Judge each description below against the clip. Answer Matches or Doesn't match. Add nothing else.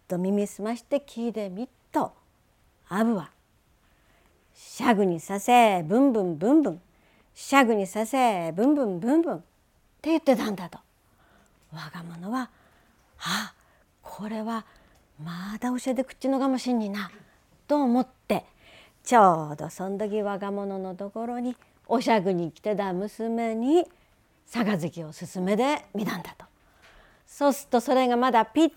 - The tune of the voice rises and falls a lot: Doesn't match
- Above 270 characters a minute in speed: Matches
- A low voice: Doesn't match